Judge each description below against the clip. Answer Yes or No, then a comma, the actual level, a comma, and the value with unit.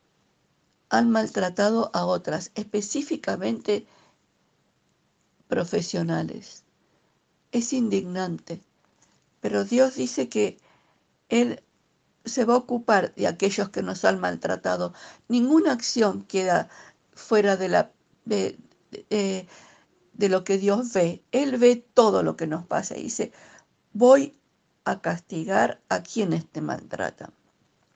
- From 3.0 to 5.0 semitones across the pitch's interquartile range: No, wide, 5.4 semitones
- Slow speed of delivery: Yes, slow, 115 wpm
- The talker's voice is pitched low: No, high, 200 Hz